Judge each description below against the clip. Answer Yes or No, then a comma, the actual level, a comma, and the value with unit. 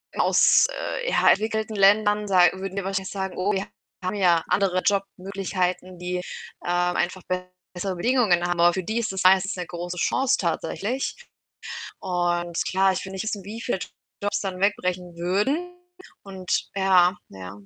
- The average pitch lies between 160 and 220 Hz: Yes, high, 190 Hz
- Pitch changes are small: Yes, narrow, 2.3 semitones